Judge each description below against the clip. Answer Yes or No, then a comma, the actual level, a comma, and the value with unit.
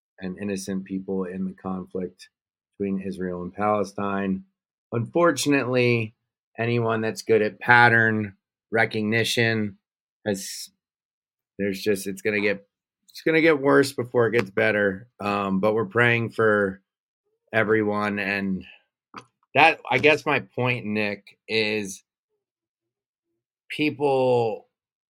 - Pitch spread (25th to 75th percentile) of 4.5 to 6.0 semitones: No, average, 3.3 semitones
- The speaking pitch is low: Yes, low, 110 Hz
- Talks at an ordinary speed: No, slow, 115 wpm